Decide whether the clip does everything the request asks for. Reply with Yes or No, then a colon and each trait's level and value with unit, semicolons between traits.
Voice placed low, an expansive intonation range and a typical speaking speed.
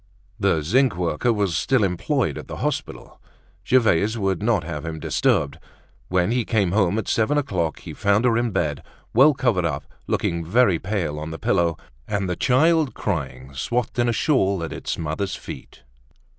Yes: low, 100 Hz; wide, 6.2 semitones; average, 175 wpm